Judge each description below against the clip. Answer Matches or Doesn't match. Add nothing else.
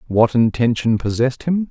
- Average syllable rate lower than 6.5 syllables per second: Matches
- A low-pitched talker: Matches